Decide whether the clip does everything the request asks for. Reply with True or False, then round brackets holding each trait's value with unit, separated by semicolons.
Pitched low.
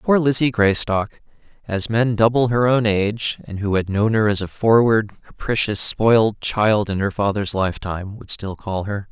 True (105 Hz)